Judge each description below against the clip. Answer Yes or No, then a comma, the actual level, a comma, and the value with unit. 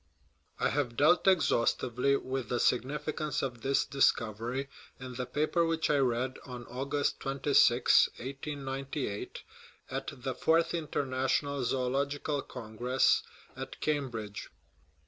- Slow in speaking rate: Yes, slow, 115 wpm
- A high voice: No, low, 135 Hz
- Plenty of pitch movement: No, narrow, 2.6 semitones